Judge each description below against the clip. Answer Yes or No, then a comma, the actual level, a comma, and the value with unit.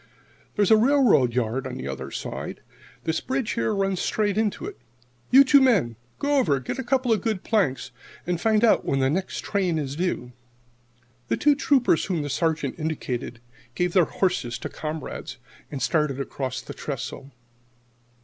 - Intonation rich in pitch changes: Yes, wide, 8.5 semitones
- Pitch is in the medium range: Yes, medium, 175 Hz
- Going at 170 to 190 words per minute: Yes, average, 180 wpm